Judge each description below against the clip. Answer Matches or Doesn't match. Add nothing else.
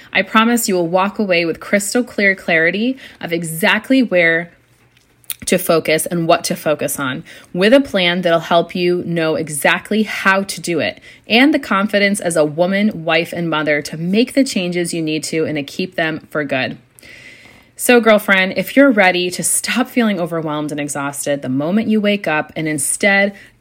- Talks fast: Doesn't match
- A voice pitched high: Doesn't match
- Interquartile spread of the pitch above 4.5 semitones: Doesn't match